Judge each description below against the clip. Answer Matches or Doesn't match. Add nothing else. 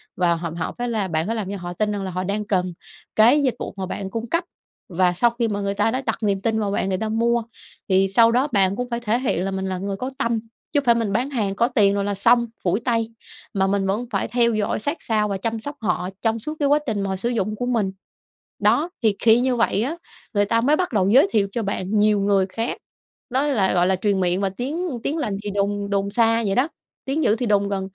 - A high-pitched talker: Matches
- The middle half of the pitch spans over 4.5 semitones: Doesn't match